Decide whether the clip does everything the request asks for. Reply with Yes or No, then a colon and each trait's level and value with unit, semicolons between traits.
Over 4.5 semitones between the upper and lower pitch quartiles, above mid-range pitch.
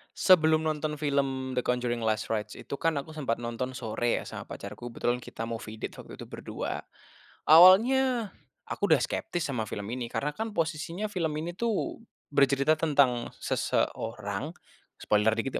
No: average, 5.3 semitones; medium, 140 Hz